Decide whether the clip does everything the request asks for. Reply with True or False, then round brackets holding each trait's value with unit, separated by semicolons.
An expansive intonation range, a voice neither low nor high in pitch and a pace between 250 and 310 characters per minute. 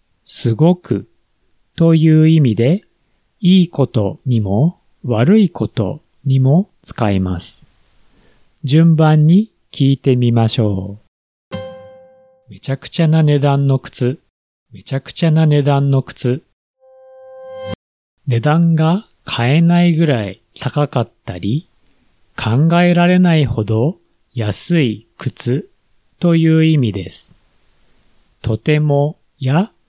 False (6.2 semitones; 145 Hz; 190 characters per minute)